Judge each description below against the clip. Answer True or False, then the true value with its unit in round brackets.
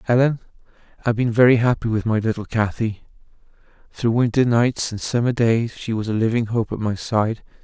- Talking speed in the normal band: True (180 wpm)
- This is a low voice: True (115 Hz)